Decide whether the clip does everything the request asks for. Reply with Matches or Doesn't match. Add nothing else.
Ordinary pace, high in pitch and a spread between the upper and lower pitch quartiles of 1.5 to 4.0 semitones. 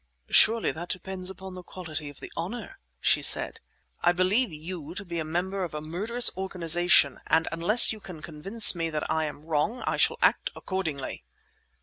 Doesn't match